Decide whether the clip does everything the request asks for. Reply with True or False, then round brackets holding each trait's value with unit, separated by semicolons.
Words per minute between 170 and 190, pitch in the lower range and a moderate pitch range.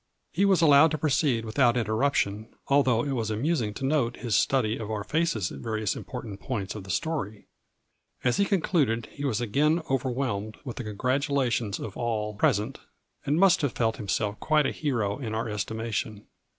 True (180 wpm; 120 Hz; 4.7 semitones)